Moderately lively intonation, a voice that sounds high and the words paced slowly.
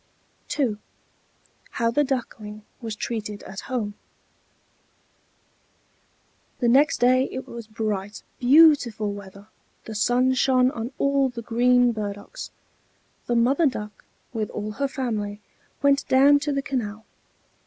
Yes: average, 3.8 semitones; high, 235 Hz; slow, 120 wpm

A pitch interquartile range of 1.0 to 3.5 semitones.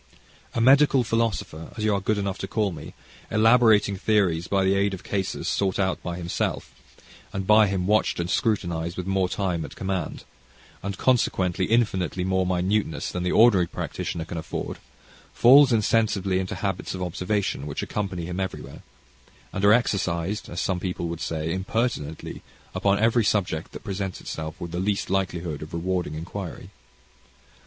Yes: average, 3.1 semitones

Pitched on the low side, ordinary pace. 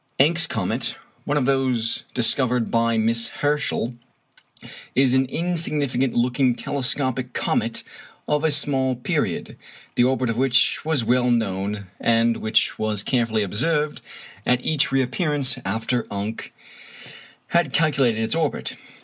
No: low, 125 Hz; slow, 125 wpm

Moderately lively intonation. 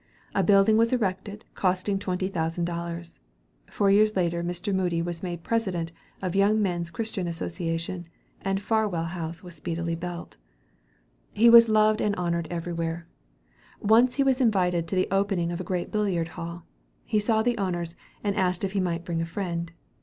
Yes: average, 3.2 semitones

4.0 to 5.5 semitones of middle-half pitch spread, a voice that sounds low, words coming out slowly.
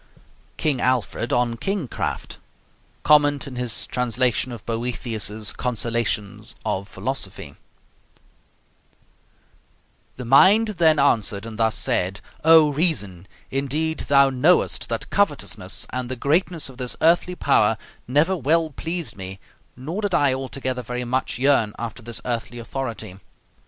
Yes: average, 4.4 semitones; low, 125 Hz; slow, 125 wpm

